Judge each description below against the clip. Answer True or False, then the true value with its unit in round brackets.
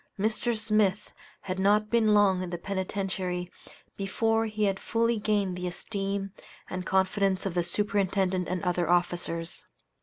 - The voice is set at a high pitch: True (195 Hz)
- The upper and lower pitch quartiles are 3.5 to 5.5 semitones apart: False (2.6 semitones)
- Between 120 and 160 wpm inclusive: True (145 wpm)